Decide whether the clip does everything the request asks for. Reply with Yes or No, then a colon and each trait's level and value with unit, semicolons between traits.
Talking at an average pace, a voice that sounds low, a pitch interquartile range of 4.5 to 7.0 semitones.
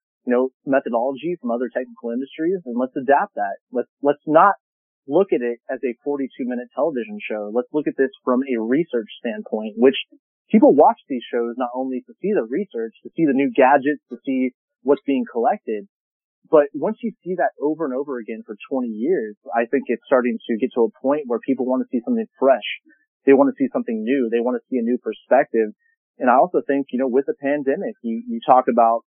No: fast, 215 wpm; low, 130 Hz; wide, 5.4 semitones